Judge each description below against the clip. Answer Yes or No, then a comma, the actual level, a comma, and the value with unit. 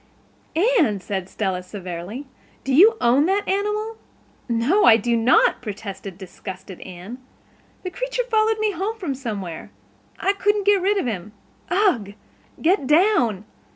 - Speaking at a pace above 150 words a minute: No, average, 140 wpm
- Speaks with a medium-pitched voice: No, very high, 265 Hz